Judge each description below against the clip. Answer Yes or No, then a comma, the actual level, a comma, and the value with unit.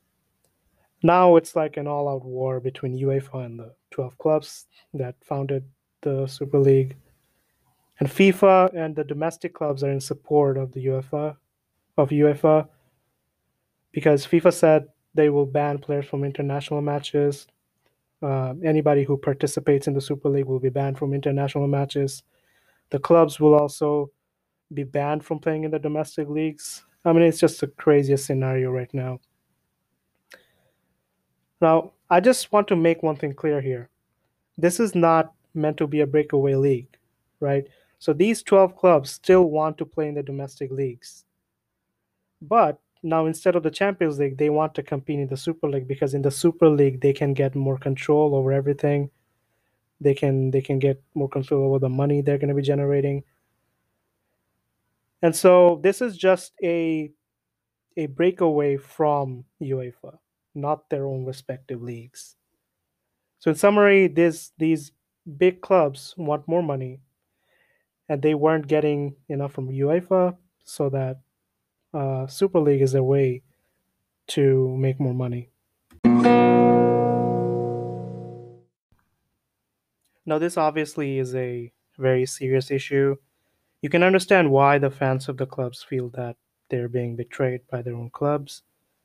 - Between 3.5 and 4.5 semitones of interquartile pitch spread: No, average, 2.8 semitones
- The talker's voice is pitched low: No, medium, 145 Hz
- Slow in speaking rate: No, average, 150 wpm